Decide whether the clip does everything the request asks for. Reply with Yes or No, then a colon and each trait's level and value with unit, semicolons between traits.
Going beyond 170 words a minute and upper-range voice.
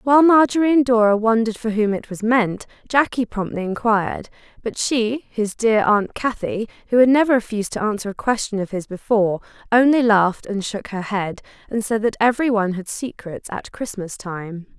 Yes: average, 180 wpm; high, 220 Hz